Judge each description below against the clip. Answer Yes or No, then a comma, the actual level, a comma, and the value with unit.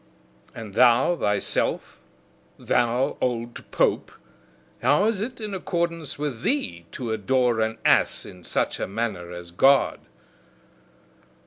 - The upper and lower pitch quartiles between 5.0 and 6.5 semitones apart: Yes, average, 5.3 semitones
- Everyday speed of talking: No, slow, 120 wpm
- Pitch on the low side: Yes, low, 120 Hz